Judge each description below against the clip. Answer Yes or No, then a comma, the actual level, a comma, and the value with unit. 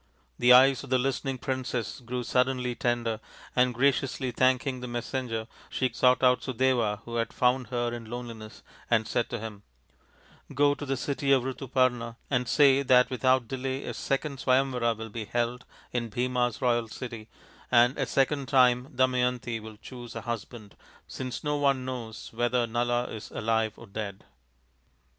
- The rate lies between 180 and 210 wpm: No, average, 170 wpm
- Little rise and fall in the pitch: Yes, narrow, 1.8 semitones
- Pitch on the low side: Yes, low, 125 Hz